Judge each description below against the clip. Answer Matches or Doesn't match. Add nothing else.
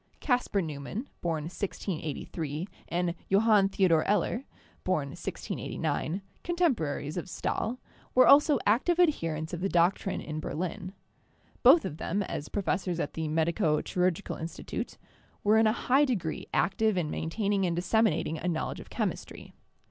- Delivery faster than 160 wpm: Doesn't match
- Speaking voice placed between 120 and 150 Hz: Doesn't match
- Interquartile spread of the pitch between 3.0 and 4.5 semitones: Doesn't match